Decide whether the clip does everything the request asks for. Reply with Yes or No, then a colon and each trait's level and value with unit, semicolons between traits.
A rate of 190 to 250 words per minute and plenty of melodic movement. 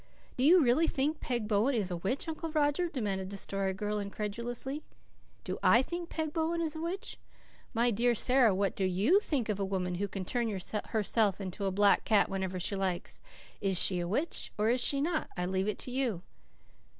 Yes: fast, 205 wpm; wide, 6.3 semitones